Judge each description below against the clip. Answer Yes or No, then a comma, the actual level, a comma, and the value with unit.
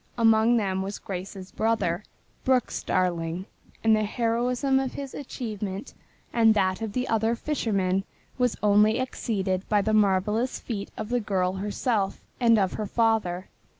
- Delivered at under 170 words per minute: Yes, average, 150 wpm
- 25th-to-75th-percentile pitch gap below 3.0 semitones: No, average, 3.3 semitones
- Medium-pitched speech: No, high, 215 Hz